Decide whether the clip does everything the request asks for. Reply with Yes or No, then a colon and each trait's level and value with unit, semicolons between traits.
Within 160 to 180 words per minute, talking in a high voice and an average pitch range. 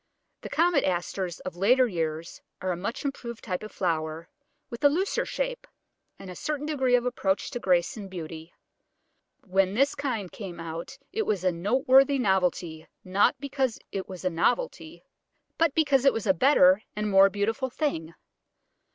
No: average, 170 wpm; high, 200 Hz; wide, 6.9 semitones